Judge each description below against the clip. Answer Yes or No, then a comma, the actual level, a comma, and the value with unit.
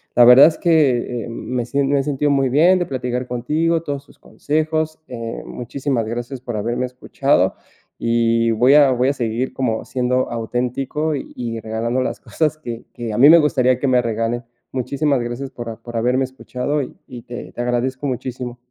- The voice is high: No, low, 125 Hz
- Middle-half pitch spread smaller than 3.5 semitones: Yes, average, 2.8 semitones